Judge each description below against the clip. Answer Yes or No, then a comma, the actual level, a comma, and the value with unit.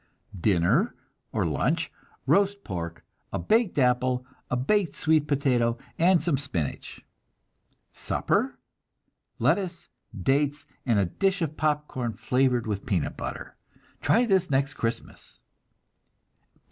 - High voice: No, medium, 140 Hz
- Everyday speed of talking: No, slow, 110 wpm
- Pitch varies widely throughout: Yes, wide, 6.6 semitones